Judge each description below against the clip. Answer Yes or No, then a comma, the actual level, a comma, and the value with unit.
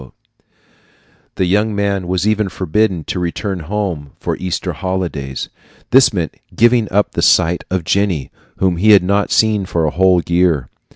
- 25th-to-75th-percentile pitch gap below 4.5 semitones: Yes, average, 3.0 semitones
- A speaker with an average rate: Yes, average, 165 wpm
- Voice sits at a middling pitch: No, very low, 95 Hz